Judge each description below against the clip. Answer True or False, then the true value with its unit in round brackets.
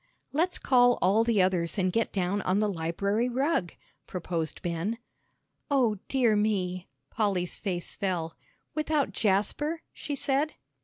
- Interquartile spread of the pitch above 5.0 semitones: True (5.6 semitones)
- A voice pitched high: True (205 Hz)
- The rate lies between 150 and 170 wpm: False (135 wpm)